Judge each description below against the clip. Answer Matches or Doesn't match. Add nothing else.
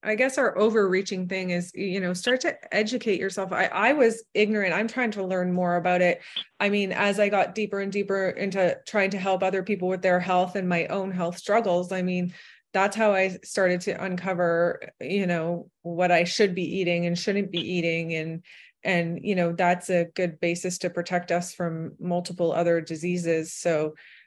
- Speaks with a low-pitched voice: Doesn't match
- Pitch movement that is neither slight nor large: Doesn't match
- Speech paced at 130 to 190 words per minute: Doesn't match